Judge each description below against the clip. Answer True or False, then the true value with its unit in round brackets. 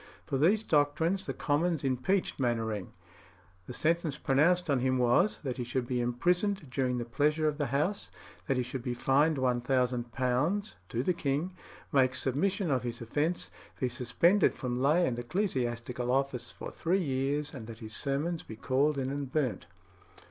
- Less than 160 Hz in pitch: True (135 Hz)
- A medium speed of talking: True (170 wpm)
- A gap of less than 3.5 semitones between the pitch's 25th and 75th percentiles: False (4.3 semitones)